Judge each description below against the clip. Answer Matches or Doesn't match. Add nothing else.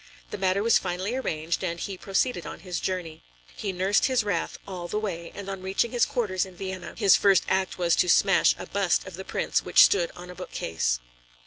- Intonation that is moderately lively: Doesn't match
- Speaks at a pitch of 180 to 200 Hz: Matches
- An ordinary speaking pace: Doesn't match